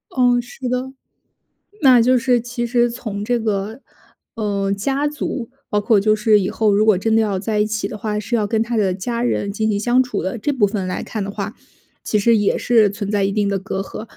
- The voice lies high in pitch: Yes, high, 215 Hz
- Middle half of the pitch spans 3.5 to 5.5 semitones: No, average, 2.9 semitones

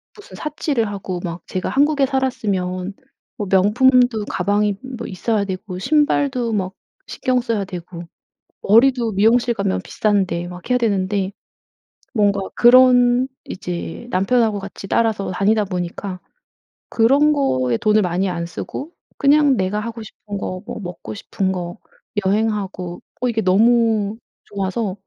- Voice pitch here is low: No, high, 205 Hz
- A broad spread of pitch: No, average, 4.4 semitones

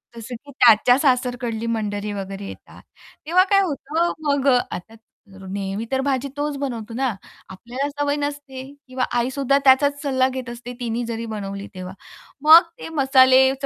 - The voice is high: Yes, very high, 255 Hz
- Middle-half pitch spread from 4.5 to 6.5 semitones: No, average, 4.0 semitones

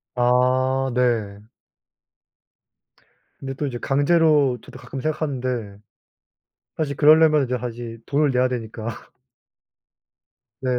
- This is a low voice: Yes, low, 130 Hz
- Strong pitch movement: No, average, 2.8 semitones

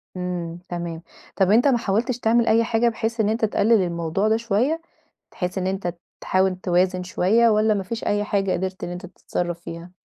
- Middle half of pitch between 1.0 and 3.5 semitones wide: No, average, 3.9 semitones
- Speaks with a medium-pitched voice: No, high, 195 Hz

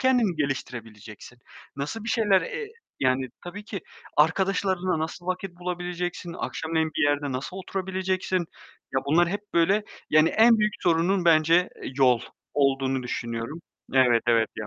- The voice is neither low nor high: Yes, medium, 170 Hz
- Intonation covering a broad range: Yes, wide, 5.7 semitones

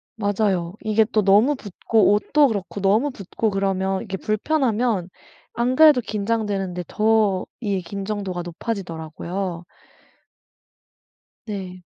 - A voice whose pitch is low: No, high, 200 Hz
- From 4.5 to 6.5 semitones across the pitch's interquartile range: No, average, 2.9 semitones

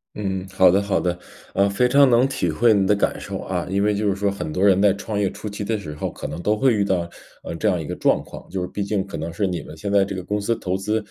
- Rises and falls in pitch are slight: Yes, narrow, 2.1 semitones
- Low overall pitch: Yes, low, 100 Hz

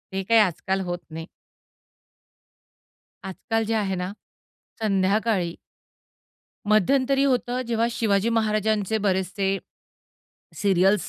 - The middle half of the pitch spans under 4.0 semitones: Yes, average, 2.9 semitones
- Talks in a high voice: Yes, high, 205 Hz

